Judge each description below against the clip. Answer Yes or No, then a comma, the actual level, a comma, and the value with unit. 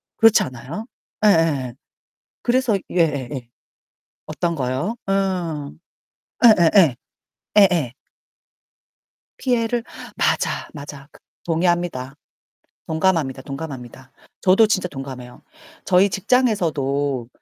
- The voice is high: No, medium, 165 Hz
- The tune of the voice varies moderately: No, wide, 6.3 semitones